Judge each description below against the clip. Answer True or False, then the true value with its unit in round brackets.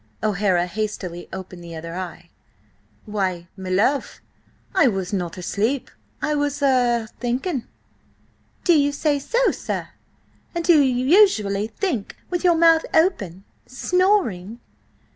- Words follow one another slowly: True (115 wpm)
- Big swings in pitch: True (8.1 semitones)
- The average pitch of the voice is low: False (235 Hz)